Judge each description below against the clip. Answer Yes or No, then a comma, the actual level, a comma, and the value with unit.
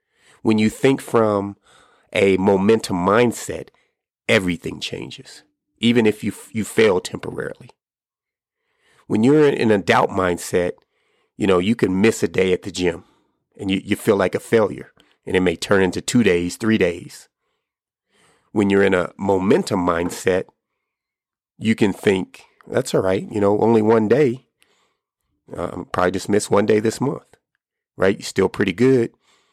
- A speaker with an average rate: Yes, average, 160 wpm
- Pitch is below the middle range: Yes, low, 105 Hz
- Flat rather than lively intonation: No, average, 3.0 semitones